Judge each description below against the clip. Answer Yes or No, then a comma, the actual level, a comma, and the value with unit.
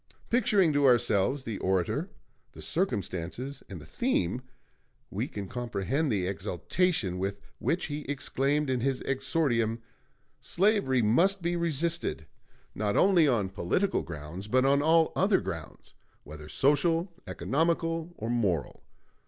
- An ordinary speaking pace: No, slow, 130 wpm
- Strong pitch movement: Yes, wide, 8.7 semitones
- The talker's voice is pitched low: Yes, low, 130 Hz